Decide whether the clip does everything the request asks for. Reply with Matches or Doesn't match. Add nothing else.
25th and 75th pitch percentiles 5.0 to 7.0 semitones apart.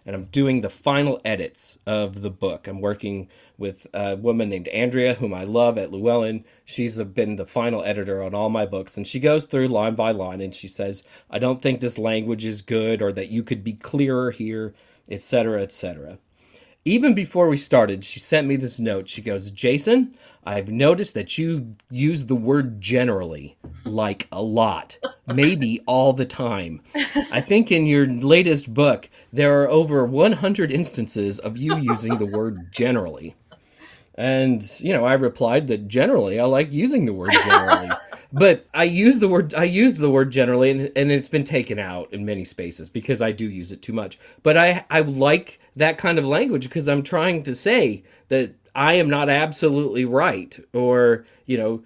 Matches